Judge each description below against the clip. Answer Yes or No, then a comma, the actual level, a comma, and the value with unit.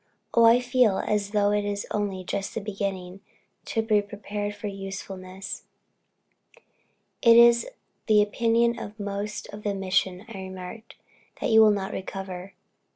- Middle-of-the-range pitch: No, high, 205 Hz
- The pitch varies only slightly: Yes, narrow, 2.3 semitones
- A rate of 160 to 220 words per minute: No, slow, 135 wpm